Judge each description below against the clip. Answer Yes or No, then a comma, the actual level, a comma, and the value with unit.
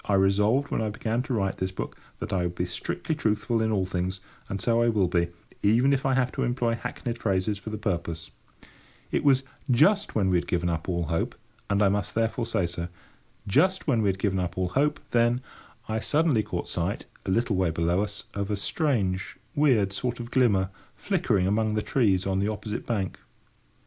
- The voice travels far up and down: No, average, 4.2 semitones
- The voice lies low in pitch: Yes, low, 105 Hz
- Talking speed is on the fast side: Yes, fast, 210 wpm